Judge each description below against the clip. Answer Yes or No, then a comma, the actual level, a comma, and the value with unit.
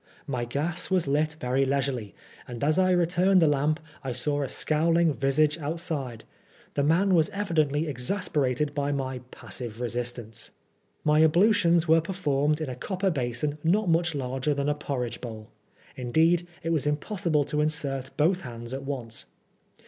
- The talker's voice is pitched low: No, medium, 150 Hz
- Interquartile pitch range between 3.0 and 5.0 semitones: Yes, average, 4.0 semitones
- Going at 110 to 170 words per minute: Yes, average, 155 wpm